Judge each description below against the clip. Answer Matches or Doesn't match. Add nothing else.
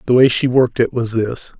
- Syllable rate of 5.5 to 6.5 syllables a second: Matches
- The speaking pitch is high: Doesn't match